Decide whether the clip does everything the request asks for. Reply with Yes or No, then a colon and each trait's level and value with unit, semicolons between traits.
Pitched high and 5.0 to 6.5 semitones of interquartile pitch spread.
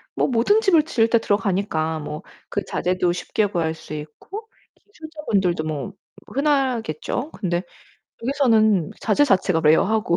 No: high, 205 Hz; wide, 7.9 semitones